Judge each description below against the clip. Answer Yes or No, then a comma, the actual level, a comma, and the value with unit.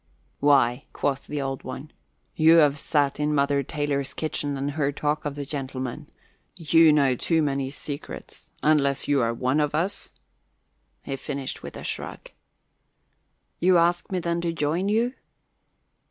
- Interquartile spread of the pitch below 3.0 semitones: Yes, narrow, 2.4 semitones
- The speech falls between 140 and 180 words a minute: Yes, average, 155 wpm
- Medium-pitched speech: Yes, medium, 145 Hz